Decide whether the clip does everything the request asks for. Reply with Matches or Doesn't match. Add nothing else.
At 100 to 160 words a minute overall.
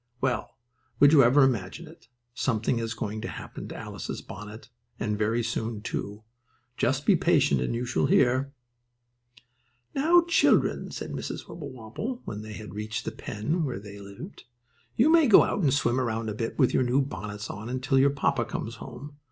Doesn't match